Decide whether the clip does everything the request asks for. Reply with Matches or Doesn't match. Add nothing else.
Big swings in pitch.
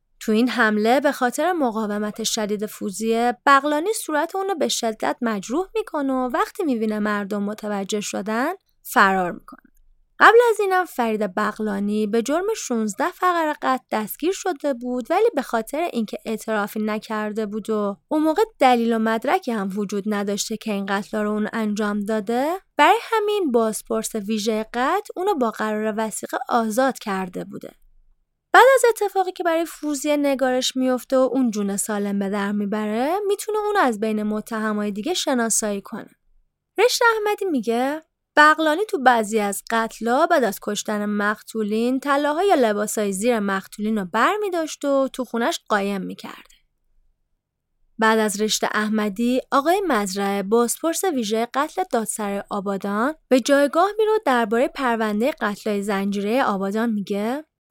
Matches